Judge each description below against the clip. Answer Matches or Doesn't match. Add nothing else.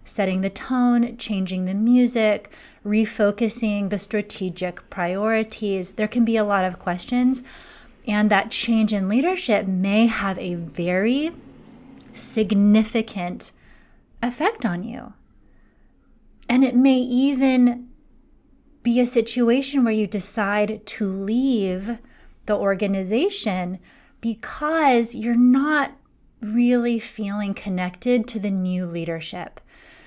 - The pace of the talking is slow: Matches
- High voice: Matches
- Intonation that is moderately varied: Matches